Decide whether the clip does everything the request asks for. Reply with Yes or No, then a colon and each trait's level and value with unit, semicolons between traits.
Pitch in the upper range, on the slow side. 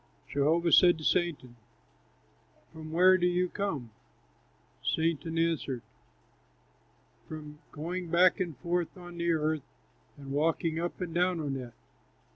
No: medium, 165 Hz; slow, 125 wpm